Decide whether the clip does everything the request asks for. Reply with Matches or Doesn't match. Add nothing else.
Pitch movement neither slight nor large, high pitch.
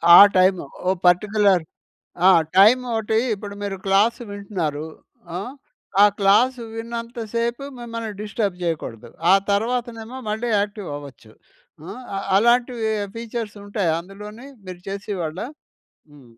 Matches